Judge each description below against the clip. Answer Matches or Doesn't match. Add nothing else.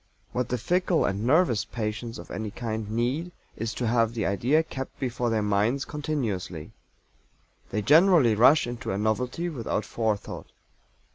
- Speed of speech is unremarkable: Matches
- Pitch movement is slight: Doesn't match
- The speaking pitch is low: Matches